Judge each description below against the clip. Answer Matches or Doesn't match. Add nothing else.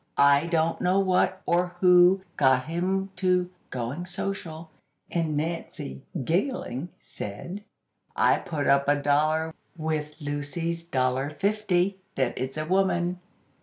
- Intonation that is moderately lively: Matches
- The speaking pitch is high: Doesn't match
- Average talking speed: Doesn't match